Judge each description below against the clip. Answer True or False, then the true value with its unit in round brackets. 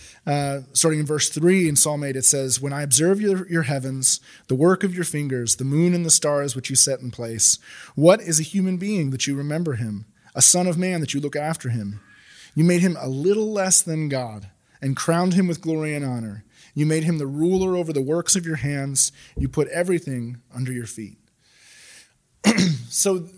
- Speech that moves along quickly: True (210 wpm)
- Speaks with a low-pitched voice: False (150 Hz)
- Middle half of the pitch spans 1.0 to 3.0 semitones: False (4.7 semitones)